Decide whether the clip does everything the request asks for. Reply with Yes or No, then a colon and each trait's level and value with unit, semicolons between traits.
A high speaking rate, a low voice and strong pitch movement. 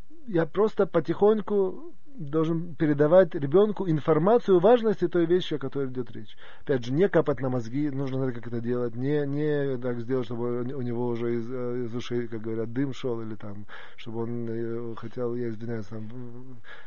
Yes: fast, 175 wpm; low, 130 Hz; wide, 5.8 semitones